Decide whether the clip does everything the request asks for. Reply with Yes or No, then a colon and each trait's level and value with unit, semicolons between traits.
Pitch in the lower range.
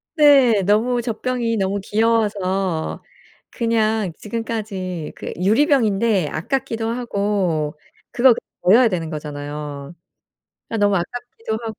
No: high, 210 Hz